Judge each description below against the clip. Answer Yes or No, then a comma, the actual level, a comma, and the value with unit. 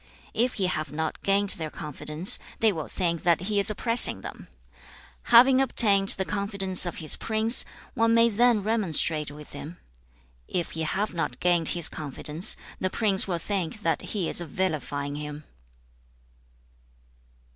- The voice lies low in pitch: No, medium, 185 Hz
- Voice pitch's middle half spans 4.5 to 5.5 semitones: Yes, average, 5.0 semitones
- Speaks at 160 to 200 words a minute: No, average, 150 wpm